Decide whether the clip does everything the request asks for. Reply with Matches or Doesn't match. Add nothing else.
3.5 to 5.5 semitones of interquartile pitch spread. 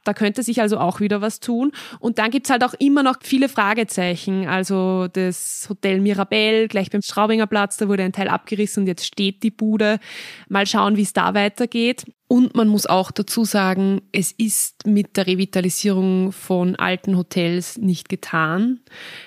Doesn't match